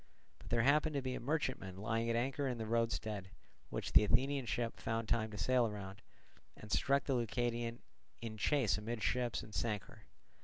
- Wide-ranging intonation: No, average, 2.9 semitones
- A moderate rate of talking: Yes, average, 185 wpm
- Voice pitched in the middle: No, low, 115 Hz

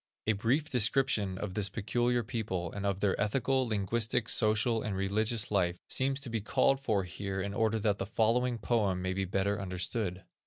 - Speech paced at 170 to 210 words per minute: Yes, average, 190 wpm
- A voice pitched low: Yes, low, 105 Hz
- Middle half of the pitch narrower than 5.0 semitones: Yes, average, 3.3 semitones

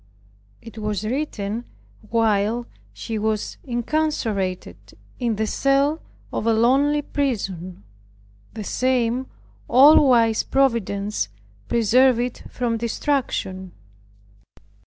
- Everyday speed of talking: No, slow, 95 wpm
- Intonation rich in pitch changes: No, average, 3.7 semitones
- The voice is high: Yes, high, 230 Hz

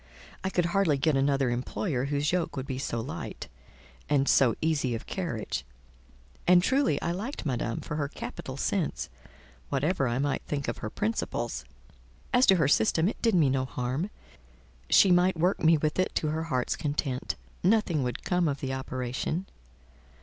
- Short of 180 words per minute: Yes, average, 170 wpm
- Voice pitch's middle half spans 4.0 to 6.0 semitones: Yes, average, 5.2 semitones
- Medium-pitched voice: Yes, medium, 145 Hz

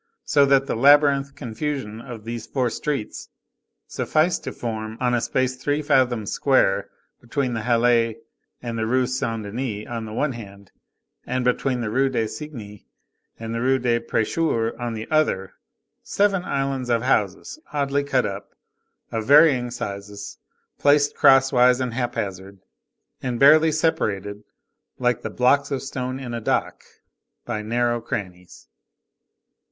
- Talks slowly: No, average, 145 wpm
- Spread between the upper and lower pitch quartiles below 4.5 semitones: Yes, average, 3.6 semitones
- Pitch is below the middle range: Yes, low, 120 Hz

